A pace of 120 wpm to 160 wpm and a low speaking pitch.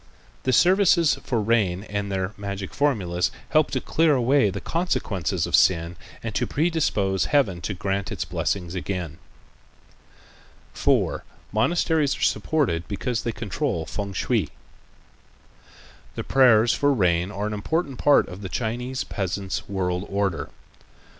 Yes: slow, 135 wpm; low, 105 Hz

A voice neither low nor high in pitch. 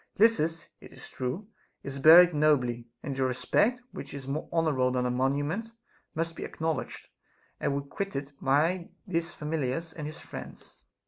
Yes: medium, 150 Hz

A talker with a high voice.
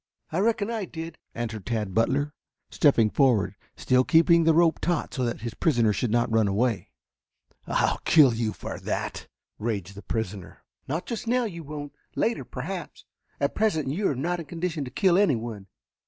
No: medium, 140 Hz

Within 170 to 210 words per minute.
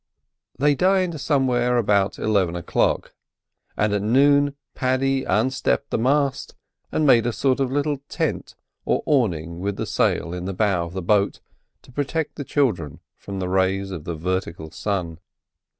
No: average, 160 wpm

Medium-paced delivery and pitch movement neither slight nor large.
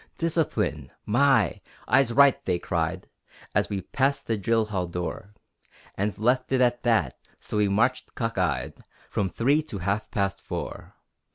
Yes: average, 155 wpm; average, 4.7 semitones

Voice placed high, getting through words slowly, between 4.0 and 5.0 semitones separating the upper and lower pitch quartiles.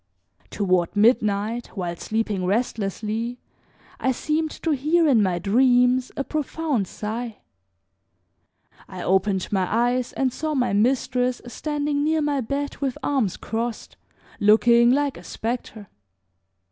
Yes: high, 240 Hz; slow, 120 wpm; average, 4.6 semitones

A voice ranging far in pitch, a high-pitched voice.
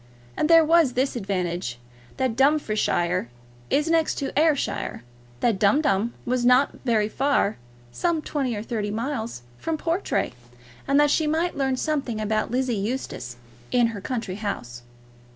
Yes: wide, 5.8 semitones; very high, 250 Hz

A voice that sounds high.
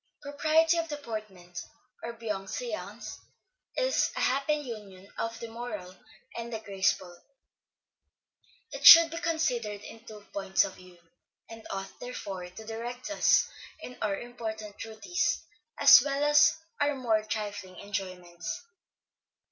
Yes: high, 225 Hz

